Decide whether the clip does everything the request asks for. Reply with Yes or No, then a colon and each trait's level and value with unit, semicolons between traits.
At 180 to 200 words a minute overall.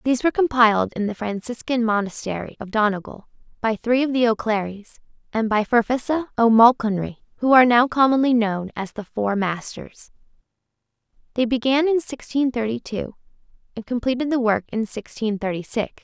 No: average, 155 wpm